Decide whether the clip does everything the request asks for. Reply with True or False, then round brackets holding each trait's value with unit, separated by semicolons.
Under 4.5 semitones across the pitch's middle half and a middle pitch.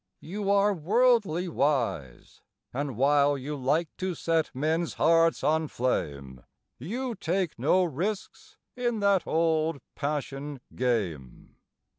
False (5.4 semitones; 155 Hz)